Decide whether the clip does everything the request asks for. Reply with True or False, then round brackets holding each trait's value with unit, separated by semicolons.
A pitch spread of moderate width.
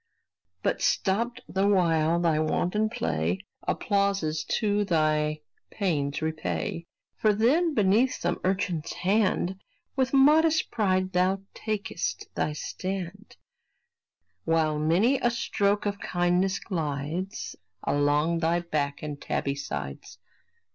True (4.8 semitones)